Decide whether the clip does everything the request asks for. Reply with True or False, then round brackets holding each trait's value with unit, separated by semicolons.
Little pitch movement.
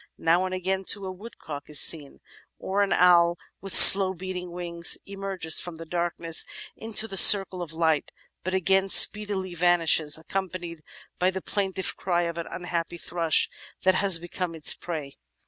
True (2.3 semitones)